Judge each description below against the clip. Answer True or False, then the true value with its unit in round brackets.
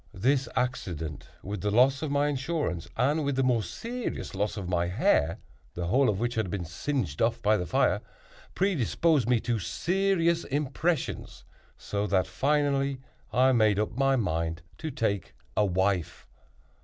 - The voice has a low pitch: True (120 Hz)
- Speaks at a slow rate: False (160 wpm)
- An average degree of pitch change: False (6.8 semitones)